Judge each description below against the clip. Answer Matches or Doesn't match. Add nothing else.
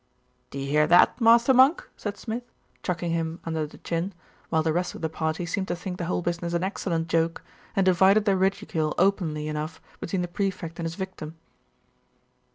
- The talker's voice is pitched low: Doesn't match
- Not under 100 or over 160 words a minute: Doesn't match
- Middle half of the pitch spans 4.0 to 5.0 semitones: Doesn't match